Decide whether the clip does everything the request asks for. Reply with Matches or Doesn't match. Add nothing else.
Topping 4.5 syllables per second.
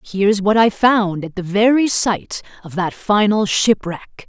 Doesn't match